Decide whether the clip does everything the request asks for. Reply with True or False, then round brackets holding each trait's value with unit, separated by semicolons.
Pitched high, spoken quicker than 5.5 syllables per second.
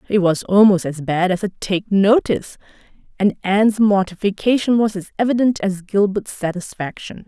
False (200 Hz; 5.1 syllables/s)